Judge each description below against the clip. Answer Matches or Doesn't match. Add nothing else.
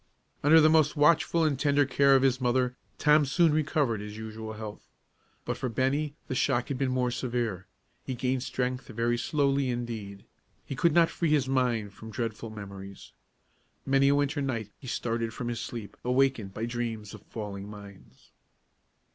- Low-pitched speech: Matches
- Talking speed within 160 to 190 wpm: Matches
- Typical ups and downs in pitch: Matches